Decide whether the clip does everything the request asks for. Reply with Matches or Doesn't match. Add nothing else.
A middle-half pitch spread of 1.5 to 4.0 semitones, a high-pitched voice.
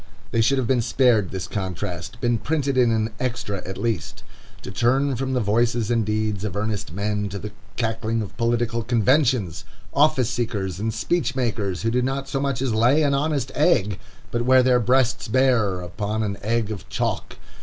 Doesn't match